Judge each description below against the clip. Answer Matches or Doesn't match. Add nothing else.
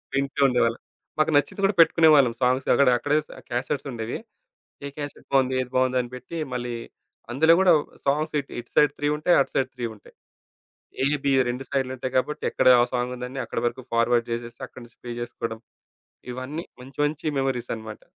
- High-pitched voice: Doesn't match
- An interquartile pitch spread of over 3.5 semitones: Doesn't match